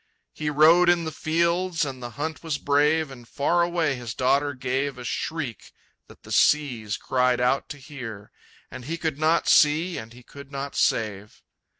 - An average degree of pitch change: Yes, average, 4.1 semitones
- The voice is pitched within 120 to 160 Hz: Yes, medium, 140 Hz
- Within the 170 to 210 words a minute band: Yes, average, 180 wpm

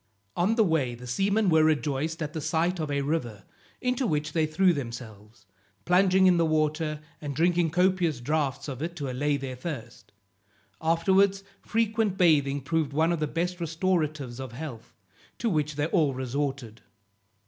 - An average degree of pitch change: Yes, average, 4.1 semitones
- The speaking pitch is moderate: Yes, medium, 155 Hz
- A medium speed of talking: Yes, average, 165 wpm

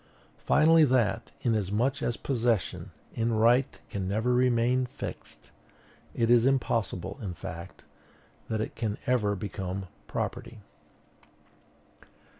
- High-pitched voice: No, low, 115 Hz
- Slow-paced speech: Yes, slow, 105 wpm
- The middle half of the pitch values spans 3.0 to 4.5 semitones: Yes, average, 3.4 semitones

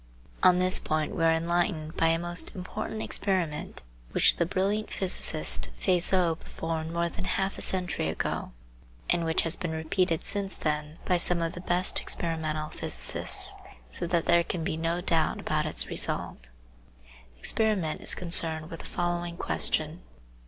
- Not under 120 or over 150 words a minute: No, average, 160 wpm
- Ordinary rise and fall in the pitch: No, narrow, 2.1 semitones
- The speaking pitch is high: No, medium, 170 Hz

